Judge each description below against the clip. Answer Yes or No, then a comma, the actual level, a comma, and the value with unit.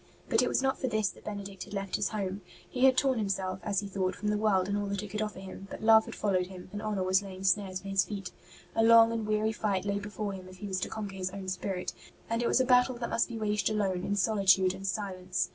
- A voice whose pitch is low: No, high, 200 Hz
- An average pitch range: No, narrow, 2.2 semitones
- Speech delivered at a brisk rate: Yes, fast, 280 wpm